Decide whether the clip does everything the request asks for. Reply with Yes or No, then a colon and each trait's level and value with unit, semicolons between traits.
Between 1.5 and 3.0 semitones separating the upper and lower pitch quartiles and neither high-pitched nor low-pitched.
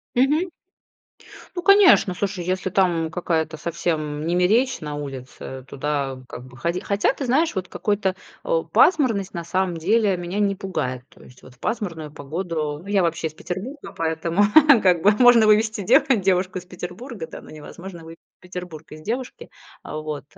No: average, 4.7 semitones; medium, 180 Hz